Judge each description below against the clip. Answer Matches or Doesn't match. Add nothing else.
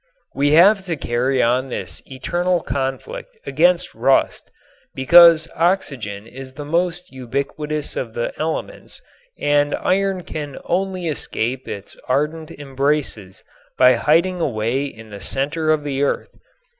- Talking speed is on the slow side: Matches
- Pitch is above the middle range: Doesn't match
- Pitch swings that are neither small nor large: Matches